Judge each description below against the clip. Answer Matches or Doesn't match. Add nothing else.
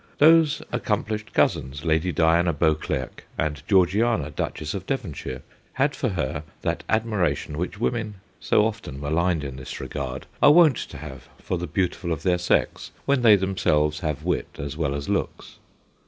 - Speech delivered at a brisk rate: Doesn't match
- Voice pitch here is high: Doesn't match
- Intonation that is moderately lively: Doesn't match